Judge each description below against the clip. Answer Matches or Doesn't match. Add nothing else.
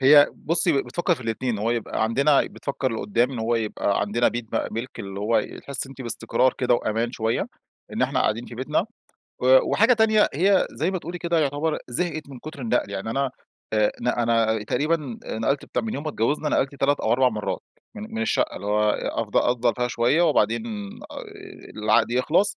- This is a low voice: Matches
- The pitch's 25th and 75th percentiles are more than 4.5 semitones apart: Matches